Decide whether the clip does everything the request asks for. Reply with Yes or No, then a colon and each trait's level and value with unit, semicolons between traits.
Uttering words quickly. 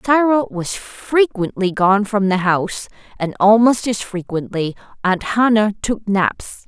No: slow, 135 wpm